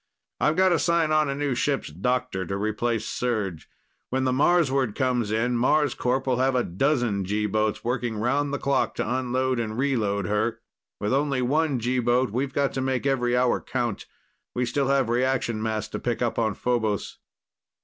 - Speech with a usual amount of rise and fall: Yes, average, 3.4 semitones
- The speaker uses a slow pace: No, average, 185 wpm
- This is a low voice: Yes, low, 125 Hz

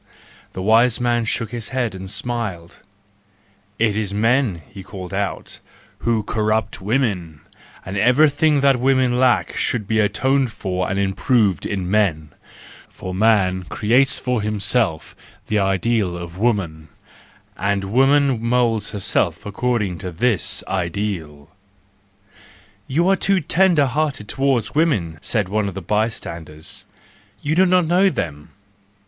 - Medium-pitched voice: No, low, 105 Hz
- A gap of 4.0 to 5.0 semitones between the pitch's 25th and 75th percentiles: Yes, average, 4.6 semitones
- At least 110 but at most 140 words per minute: Yes, slow, 135 wpm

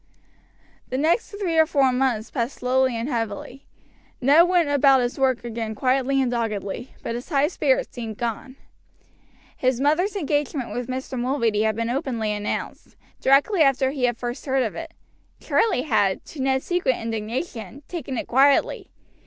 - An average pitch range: Yes, average, 3.4 semitones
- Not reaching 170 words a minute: Yes, average, 160 wpm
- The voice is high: Yes, very high, 260 Hz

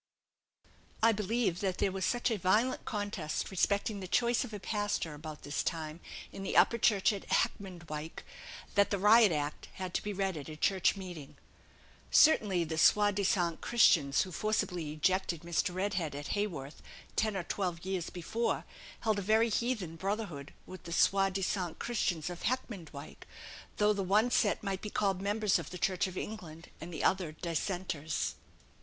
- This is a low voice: No, high, 190 Hz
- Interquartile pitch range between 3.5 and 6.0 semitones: Yes, average, 3.8 semitones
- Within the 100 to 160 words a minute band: No, average, 170 wpm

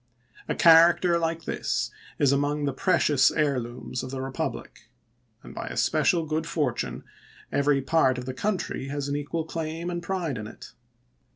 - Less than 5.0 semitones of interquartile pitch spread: Yes, average, 3.8 semitones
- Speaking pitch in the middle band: Yes, medium, 145 Hz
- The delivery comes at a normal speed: Yes, average, 175 wpm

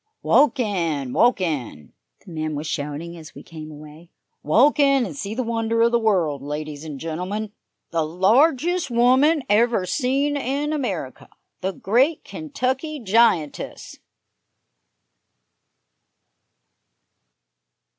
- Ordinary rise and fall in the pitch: No, wide, 8.5 semitones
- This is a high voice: Yes, high, 205 Hz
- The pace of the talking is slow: Yes, slow, 115 wpm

